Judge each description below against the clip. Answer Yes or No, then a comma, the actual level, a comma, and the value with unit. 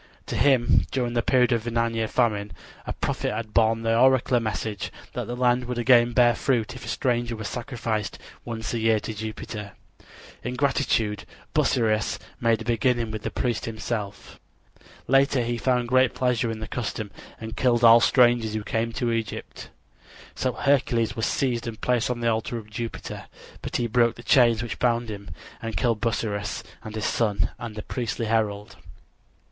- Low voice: Yes, low, 115 Hz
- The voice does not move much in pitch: Yes, narrow, 1.8 semitones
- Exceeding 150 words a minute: Yes, average, 180 wpm